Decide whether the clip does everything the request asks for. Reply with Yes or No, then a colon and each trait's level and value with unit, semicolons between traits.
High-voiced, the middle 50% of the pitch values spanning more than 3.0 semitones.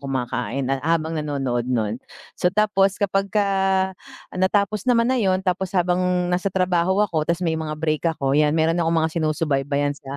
No: medium, 165 Hz; average, 4.7 semitones